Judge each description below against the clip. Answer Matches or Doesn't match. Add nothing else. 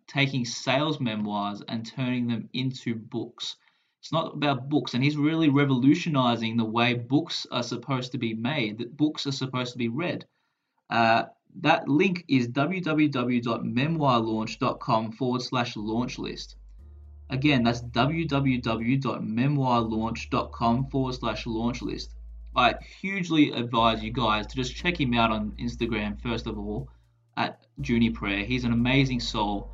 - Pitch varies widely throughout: Doesn't match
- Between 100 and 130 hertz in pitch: Matches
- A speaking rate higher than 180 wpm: Doesn't match